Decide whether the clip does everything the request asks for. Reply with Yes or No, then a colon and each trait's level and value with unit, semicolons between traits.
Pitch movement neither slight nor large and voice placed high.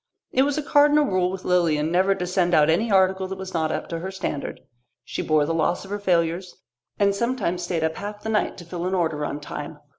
No: average, 3.1 semitones; medium, 180 Hz